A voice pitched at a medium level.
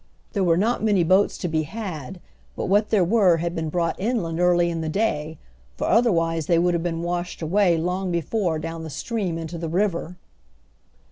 Yes: medium, 175 Hz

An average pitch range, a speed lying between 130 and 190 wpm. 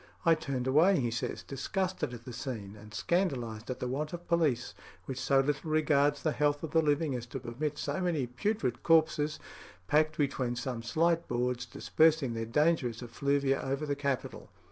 Yes: average, 4.1 semitones; average, 180 wpm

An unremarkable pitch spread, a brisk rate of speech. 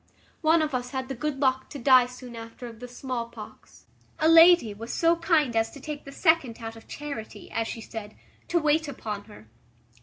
Yes: average, 4.9 semitones; fast, 210 wpm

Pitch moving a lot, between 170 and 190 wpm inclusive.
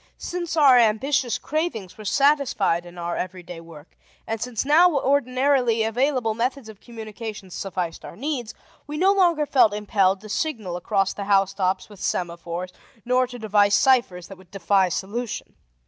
No: wide, 5.7 semitones; average, 160 wpm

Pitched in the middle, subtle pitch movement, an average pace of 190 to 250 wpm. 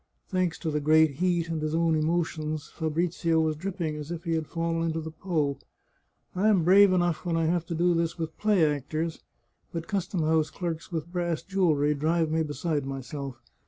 Yes: medium, 165 Hz; narrow, 1.9 semitones; average, 195 wpm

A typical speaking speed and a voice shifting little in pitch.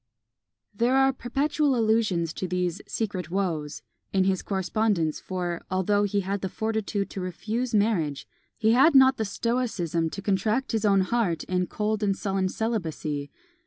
No: average, 155 wpm; average, 3.6 semitones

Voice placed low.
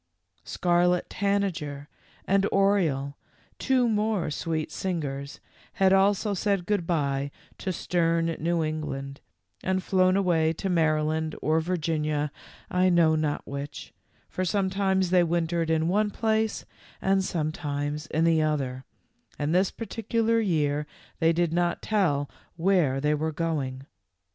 No: medium, 165 Hz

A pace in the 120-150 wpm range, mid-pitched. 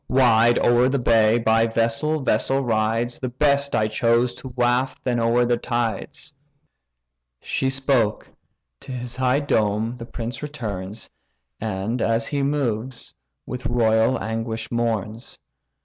No: slow, 135 wpm; low, 120 Hz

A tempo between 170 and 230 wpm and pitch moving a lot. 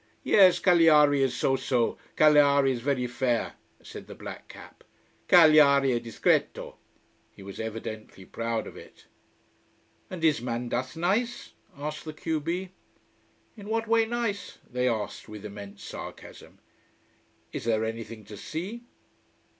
No: slow, 135 wpm; wide, 6.4 semitones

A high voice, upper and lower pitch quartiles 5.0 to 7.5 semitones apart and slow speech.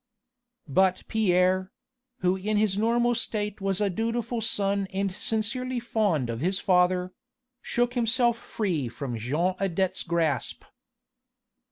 No: high, 195 Hz; average, 3.8 semitones; slow, 125 wpm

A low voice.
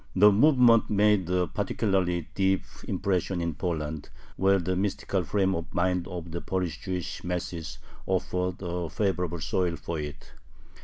Yes: very low, 90 Hz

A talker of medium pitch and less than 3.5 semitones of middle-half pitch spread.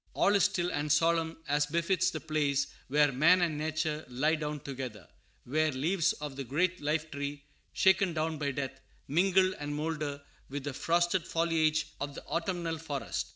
Yes: medium, 155 Hz; average, 2.8 semitones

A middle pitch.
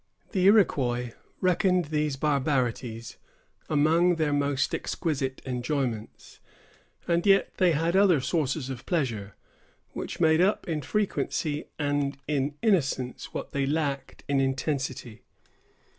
Yes: medium, 145 Hz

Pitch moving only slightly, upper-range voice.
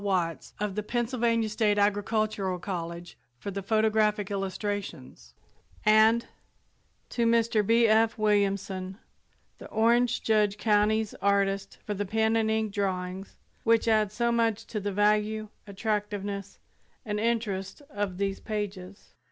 Yes: narrow, 1.9 semitones; high, 210 Hz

